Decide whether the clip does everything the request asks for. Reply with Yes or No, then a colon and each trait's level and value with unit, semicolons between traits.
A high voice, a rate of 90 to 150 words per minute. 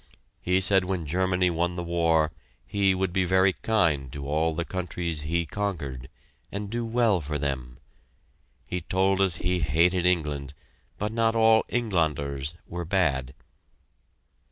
No: very low, 85 Hz; average, 145 wpm